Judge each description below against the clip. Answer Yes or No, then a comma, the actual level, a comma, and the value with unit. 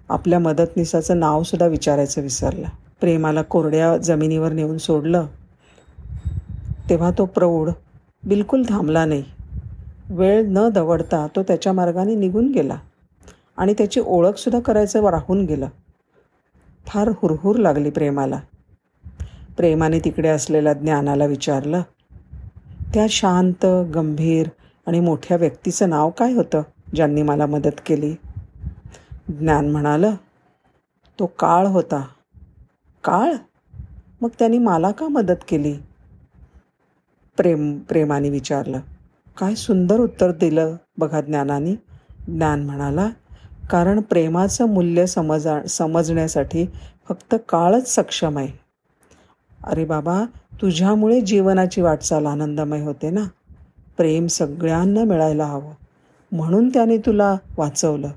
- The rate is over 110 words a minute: No, average, 105 wpm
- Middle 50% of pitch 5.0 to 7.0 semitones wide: No, average, 4.3 semitones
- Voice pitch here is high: No, medium, 165 Hz